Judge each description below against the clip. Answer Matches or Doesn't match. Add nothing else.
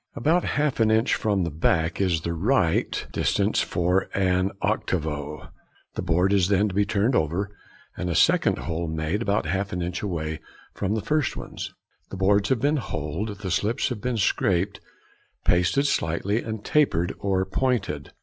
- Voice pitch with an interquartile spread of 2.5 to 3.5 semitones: Doesn't match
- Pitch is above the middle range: Doesn't match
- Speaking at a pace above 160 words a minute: Matches